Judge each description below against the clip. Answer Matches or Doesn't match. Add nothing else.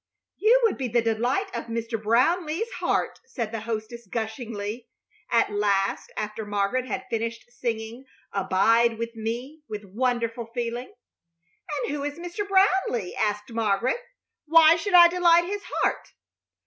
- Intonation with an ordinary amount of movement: Doesn't match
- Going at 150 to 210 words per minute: Doesn't match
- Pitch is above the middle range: Matches